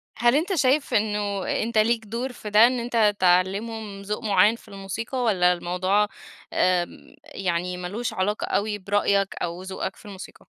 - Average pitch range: Yes, average, 3.2 semitones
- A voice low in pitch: No, high, 205 Hz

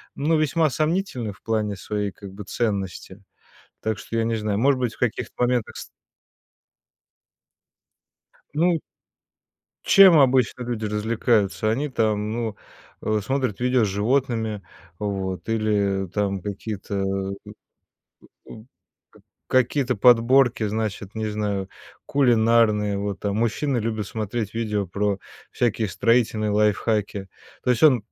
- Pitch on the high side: No, low, 110 Hz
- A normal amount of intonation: Yes, average, 3.2 semitones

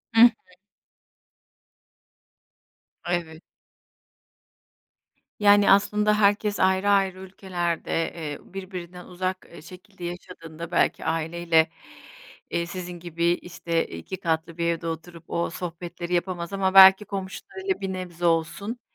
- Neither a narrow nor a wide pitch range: No, narrow, 2.2 semitones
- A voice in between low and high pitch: Yes, medium, 175 Hz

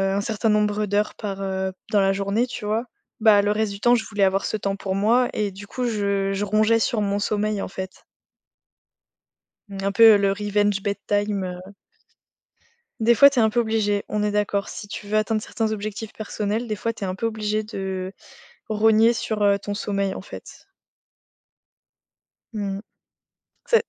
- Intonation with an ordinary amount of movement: No, narrow, 1.5 semitones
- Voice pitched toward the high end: Yes, high, 210 Hz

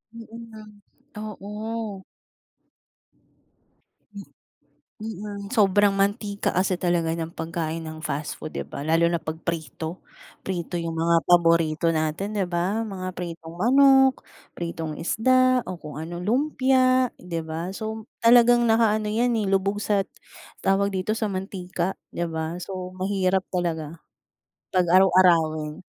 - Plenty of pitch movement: No, average, 4.3 semitones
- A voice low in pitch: No, medium, 185 Hz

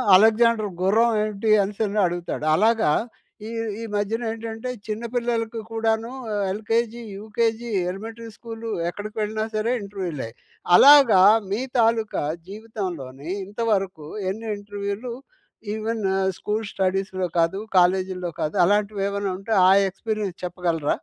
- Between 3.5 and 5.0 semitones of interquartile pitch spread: No, average, 2.8 semitones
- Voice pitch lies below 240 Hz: Yes, high, 210 Hz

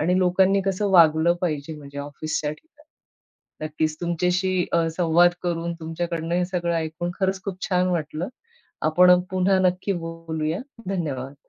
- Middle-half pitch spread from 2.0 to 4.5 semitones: Yes, narrow, 2.5 semitones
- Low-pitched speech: No, medium, 170 Hz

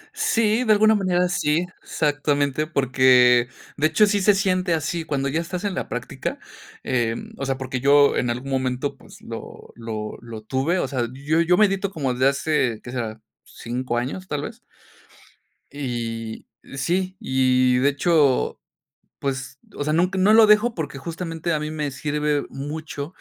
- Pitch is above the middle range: No, medium, 145 Hz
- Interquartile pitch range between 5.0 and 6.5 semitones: Yes, wide, 5.4 semitones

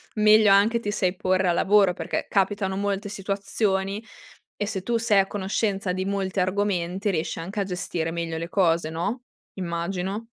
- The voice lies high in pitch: Yes, high, 195 Hz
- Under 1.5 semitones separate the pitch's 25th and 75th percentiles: No, narrow, 2.2 semitones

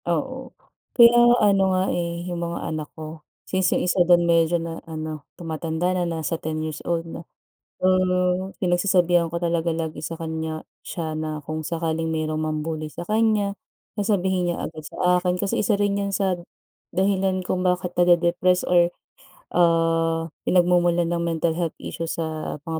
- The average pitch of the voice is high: No, medium, 170 Hz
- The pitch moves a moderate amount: No, narrow, 2.1 semitones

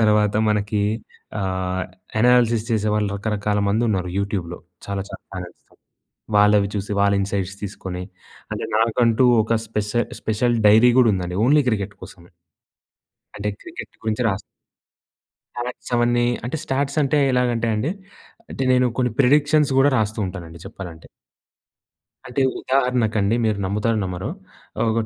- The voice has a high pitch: No, low, 105 Hz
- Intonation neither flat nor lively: Yes, average, 3.4 semitones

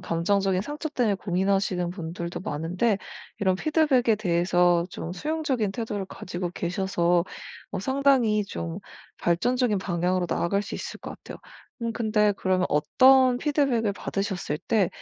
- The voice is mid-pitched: No, high, 195 Hz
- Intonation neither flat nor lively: Yes, average, 4.9 semitones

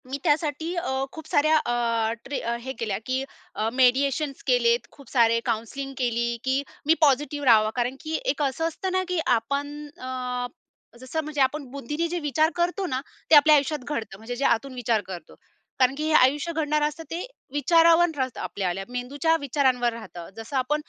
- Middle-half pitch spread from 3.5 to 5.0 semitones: Yes, average, 3.9 semitones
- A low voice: No, very high, 275 Hz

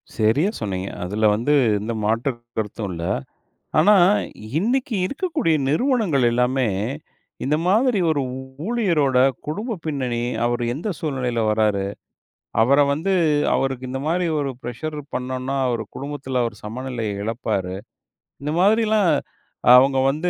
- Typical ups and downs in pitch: No, wide, 6.3 semitones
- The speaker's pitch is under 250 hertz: Yes, low, 135 Hz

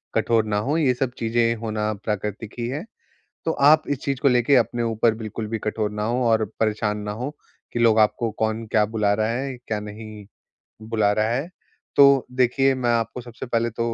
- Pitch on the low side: Yes, low, 115 Hz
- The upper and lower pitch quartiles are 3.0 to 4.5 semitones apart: No, narrow, 2.4 semitones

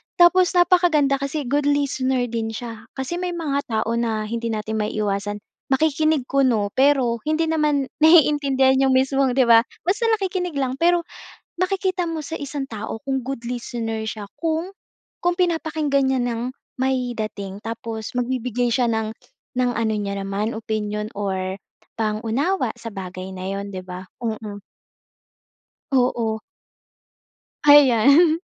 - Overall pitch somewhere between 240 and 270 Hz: Yes, very high, 255 Hz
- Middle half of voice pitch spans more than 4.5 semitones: Yes, wide, 5.4 semitones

